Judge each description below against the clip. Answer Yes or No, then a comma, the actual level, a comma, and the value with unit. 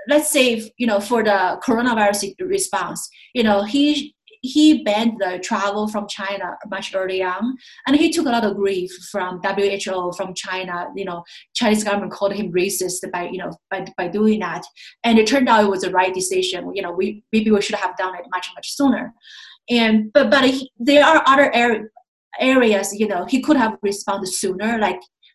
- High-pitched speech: Yes, high, 210 Hz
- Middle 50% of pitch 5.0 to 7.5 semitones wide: No, average, 4.4 semitones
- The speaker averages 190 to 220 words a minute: Yes, average, 200 wpm